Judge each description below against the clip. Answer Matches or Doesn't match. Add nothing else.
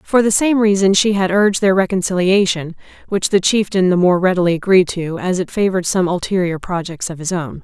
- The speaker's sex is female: Matches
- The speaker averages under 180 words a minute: Doesn't match